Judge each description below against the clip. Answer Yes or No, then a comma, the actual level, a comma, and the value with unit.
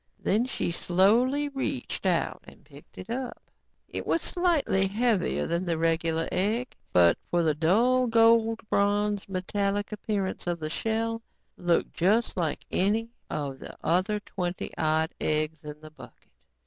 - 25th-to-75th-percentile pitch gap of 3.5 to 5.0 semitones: No, wide, 5.5 semitones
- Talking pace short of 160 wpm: Yes, average, 150 wpm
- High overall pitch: Yes, high, 195 Hz